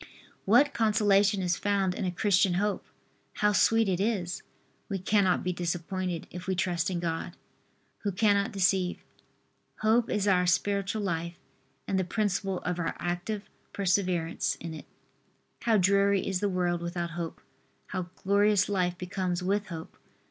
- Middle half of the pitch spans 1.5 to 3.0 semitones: Yes, narrow, 2.4 semitones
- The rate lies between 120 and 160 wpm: Yes, average, 150 wpm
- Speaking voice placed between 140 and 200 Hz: Yes, high, 190 Hz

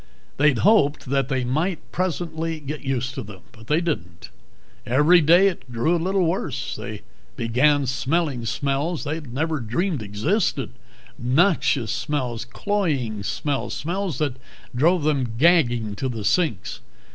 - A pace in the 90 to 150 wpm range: Yes, slow, 135 wpm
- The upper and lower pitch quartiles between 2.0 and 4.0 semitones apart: No, average, 5.3 semitones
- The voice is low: No, medium, 145 Hz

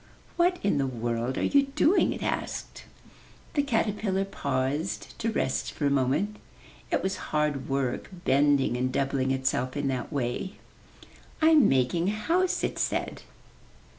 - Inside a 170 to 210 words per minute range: No, average, 145 wpm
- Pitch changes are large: Yes, wide, 8.0 semitones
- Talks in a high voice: No, medium, 145 Hz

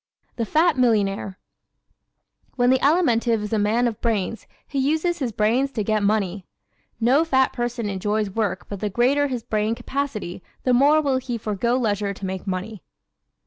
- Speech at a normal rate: Yes, average, 175 wpm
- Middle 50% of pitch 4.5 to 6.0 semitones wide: No, average, 4.0 semitones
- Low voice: No, high, 230 Hz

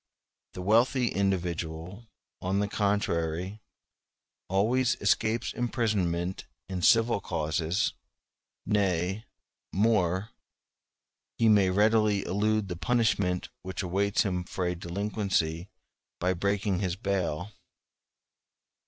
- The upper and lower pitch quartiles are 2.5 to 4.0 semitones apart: Yes, average, 3.1 semitones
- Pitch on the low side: Yes, very low, 95 Hz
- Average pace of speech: No, slow, 95 wpm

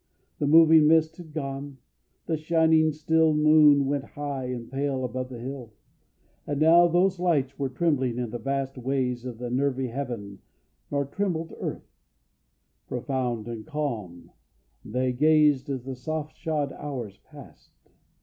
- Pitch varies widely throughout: No, average, 3.6 semitones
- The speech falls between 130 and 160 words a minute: Yes, average, 150 wpm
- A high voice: No, medium, 140 Hz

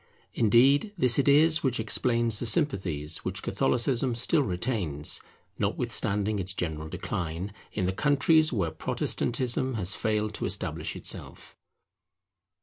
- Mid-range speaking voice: No, low, 110 Hz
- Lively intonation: Yes, wide, 6.3 semitones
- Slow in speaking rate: Yes, slow, 125 wpm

